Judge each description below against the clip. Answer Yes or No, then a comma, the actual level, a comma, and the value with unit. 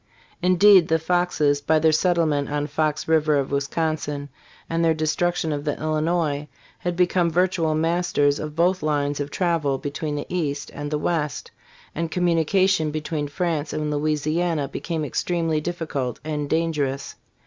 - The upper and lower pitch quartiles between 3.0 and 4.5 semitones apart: No, narrow, 2.5 semitones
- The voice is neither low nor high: Yes, medium, 155 Hz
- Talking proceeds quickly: No, average, 155 wpm